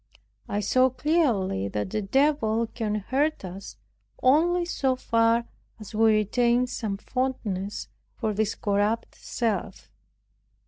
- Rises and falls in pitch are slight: No, average, 4.0 semitones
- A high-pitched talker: Yes, high, 225 Hz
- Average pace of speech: No, slow, 120 wpm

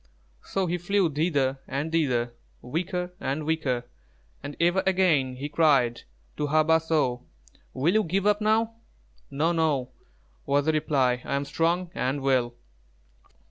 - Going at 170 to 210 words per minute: No, average, 150 wpm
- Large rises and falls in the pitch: No, average, 4.6 semitones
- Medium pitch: Yes, medium, 155 Hz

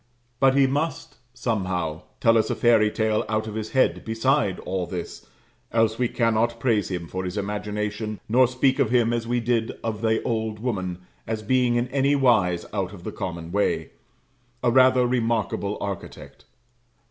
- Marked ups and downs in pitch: No, average, 3.2 semitones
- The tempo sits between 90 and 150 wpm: No, average, 170 wpm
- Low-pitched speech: Yes, low, 110 Hz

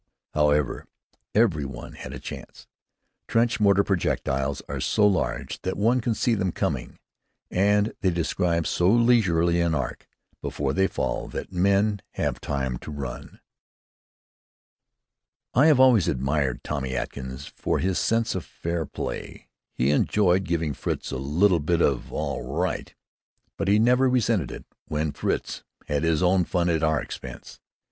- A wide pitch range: Yes, wide, 6.0 semitones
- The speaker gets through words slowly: No, average, 150 wpm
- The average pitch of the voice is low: Yes, very low, 85 Hz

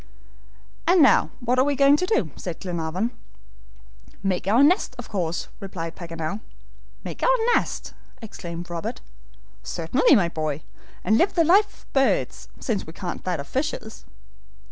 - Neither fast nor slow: Yes, average, 150 wpm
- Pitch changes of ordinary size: No, wide, 8.4 semitones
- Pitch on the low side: No, high, 200 Hz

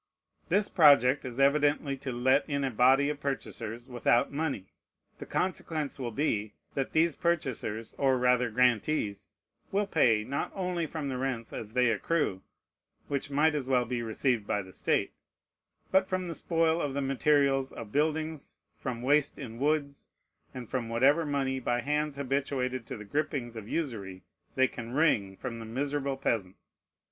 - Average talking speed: Yes, average, 165 wpm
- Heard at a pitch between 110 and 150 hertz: Yes, low, 135 Hz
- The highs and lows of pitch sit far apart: No, average, 3.8 semitones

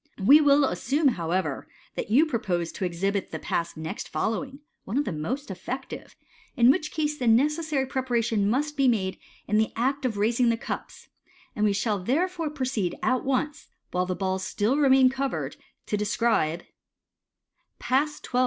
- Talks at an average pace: Yes, average, 170 wpm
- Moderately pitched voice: No, high, 245 Hz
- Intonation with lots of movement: Yes, wide, 5.8 semitones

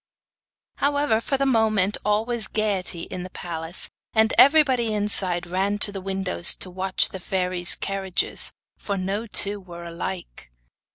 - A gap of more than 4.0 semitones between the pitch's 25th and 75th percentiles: No, average, 3.1 semitones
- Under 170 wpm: Yes, average, 150 wpm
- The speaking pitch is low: No, high, 195 Hz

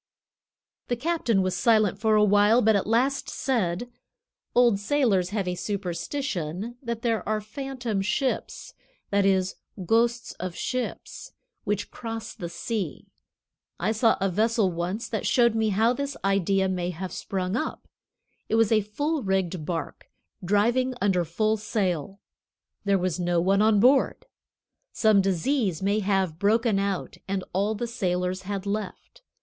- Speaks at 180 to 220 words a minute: No, average, 150 wpm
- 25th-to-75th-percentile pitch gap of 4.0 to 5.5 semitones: No, average, 3.6 semitones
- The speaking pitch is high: Yes, high, 205 Hz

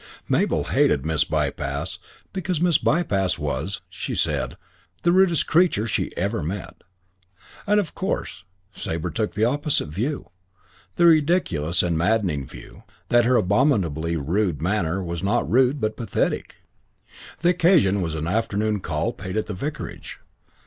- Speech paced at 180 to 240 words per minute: No, average, 140 wpm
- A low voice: Yes, low, 105 Hz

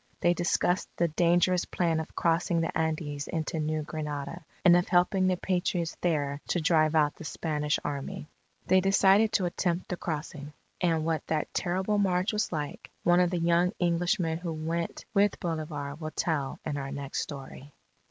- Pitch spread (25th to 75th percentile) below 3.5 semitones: Yes, narrow, 2.6 semitones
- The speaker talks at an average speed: Yes, average, 170 wpm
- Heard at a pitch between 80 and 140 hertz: No, medium, 165 Hz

